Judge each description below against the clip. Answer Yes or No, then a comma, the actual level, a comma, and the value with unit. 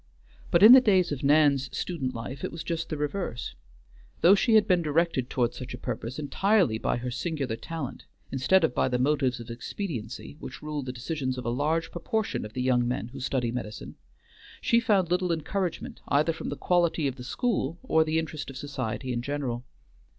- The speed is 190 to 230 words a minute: Yes, average, 200 wpm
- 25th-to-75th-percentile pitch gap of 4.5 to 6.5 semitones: Yes, average, 5.2 semitones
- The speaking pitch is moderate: Yes, medium, 145 Hz